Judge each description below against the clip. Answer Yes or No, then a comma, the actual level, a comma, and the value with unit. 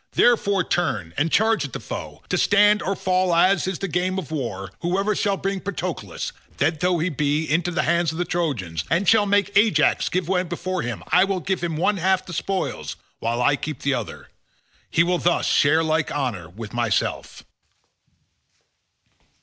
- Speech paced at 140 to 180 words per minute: No, average, 190 wpm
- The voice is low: No, medium, 175 Hz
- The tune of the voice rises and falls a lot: No, average, 4.5 semitones